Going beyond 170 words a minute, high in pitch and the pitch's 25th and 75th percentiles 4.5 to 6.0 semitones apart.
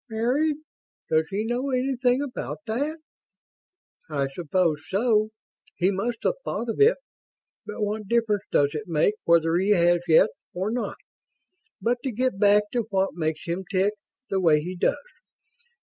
No: average, 155 wpm; high, 205 Hz; wide, 5.6 semitones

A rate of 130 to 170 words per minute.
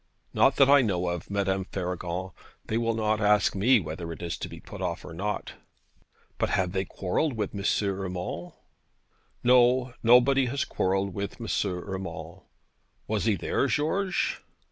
Yes: average, 160 wpm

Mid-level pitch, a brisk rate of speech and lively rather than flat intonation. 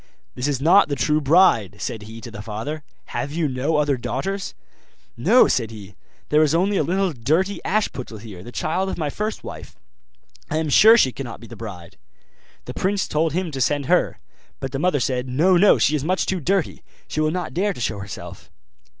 Yes: medium, 150 Hz; fast, 210 wpm; wide, 6.8 semitones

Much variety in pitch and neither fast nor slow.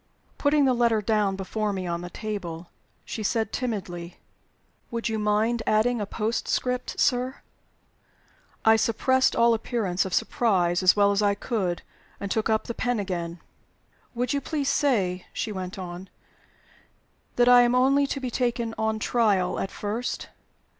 No: average, 4.1 semitones; average, 155 wpm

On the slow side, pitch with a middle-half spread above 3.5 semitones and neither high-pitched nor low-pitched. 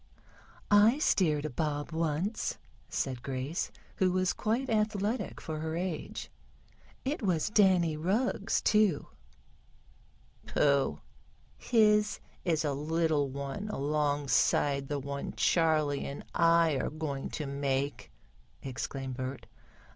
Yes: slow, 110 wpm; average, 5.3 semitones; medium, 155 Hz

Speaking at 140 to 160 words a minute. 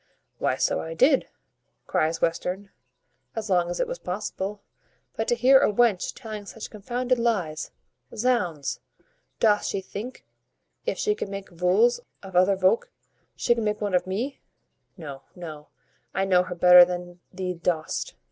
Yes: average, 155 wpm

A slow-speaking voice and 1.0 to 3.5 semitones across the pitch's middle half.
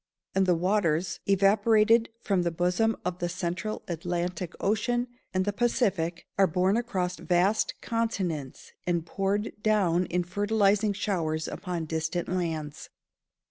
Yes: slow, 130 wpm; average, 3.2 semitones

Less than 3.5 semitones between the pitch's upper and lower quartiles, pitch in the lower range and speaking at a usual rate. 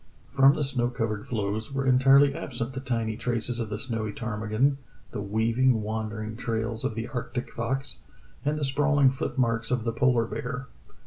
Yes: average, 3.1 semitones; low, 120 Hz; average, 175 wpm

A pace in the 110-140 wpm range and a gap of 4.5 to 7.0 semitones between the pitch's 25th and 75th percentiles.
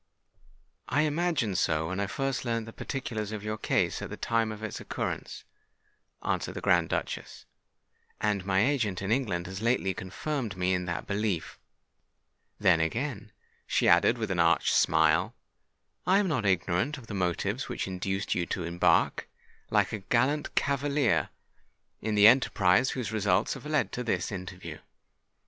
No: average, 160 wpm; average, 5.3 semitones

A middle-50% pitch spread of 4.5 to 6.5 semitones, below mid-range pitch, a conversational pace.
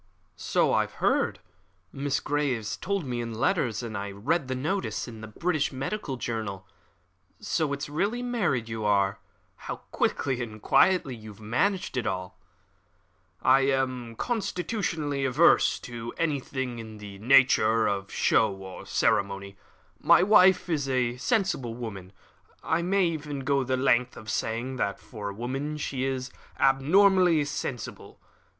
Yes: wide, 5.4 semitones; low, 130 Hz; average, 145 wpm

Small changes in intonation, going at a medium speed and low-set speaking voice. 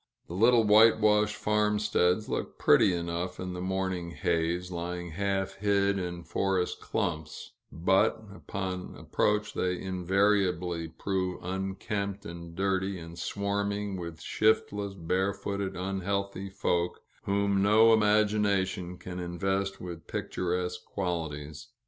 No: narrow, 2.2 semitones; slow, 110 wpm; very low, 95 Hz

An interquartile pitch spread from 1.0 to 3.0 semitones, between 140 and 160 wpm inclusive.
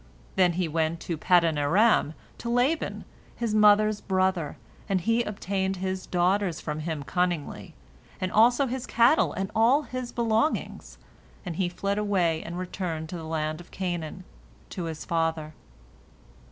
No: average, 4.5 semitones; average, 150 wpm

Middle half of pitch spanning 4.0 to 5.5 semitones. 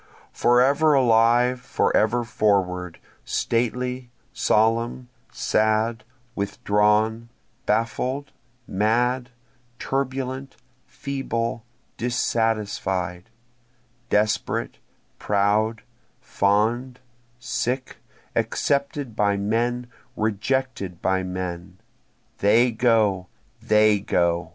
No: average, 3.3 semitones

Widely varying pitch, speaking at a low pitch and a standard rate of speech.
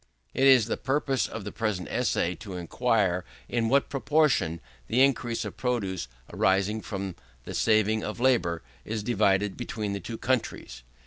No: average, 4.4 semitones; low, 110 Hz; average, 155 wpm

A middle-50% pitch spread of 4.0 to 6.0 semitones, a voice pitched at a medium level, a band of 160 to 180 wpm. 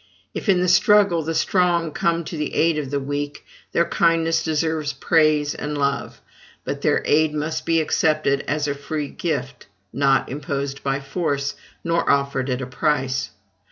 No: average, 2.9 semitones; medium, 150 Hz; average, 165 wpm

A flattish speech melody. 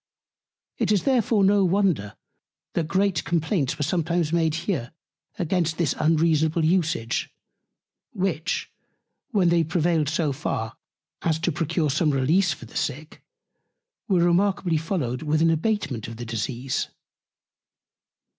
No: average, 3.3 semitones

